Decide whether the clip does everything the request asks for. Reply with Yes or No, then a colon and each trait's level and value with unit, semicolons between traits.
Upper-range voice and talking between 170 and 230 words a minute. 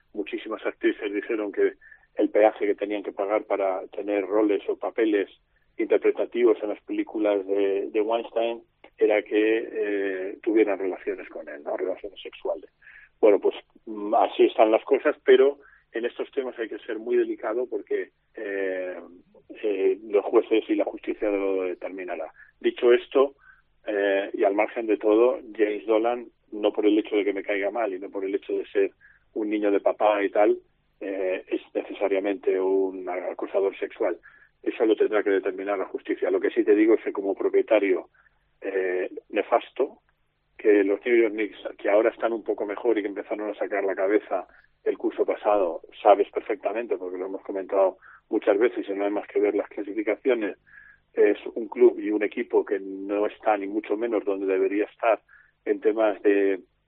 Yes: very high, 345 Hz; average, 175 wpm